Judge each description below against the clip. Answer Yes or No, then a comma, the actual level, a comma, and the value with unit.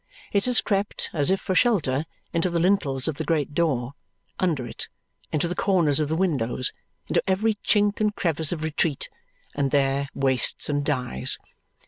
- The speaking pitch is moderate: Yes, medium, 155 Hz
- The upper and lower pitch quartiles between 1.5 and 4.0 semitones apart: No, average, 5.2 semitones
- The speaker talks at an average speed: Yes, average, 170 wpm